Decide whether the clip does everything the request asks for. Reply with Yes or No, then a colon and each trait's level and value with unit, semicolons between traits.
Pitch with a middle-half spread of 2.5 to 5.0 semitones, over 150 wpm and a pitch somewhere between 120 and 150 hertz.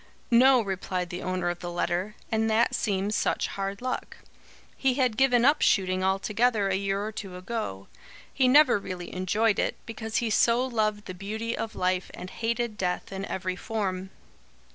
No: average, 3.9 semitones; average, 175 wpm; high, 205 Hz